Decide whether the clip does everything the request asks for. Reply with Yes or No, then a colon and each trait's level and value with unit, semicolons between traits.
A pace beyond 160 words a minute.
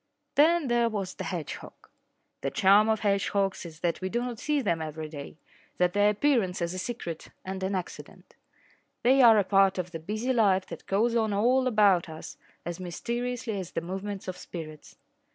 Yes: average, 190 wpm